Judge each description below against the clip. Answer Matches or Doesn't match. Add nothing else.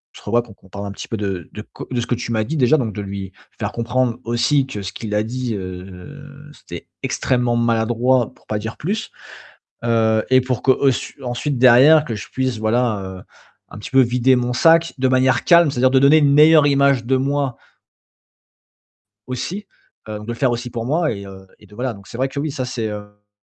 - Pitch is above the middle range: Doesn't match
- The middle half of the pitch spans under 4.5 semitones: Matches